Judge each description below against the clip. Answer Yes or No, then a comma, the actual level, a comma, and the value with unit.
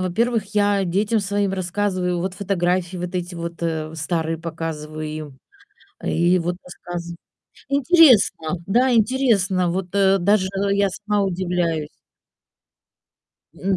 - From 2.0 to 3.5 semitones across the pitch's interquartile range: Yes, average, 2.9 semitones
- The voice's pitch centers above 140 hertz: Yes, medium, 185 Hz